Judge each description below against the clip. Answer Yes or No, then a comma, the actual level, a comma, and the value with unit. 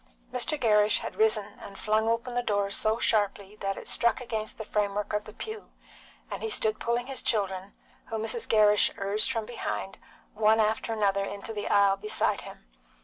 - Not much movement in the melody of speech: Yes, narrow, 2.0 semitones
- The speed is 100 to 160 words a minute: No, average, 190 wpm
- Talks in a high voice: Yes, high, 215 Hz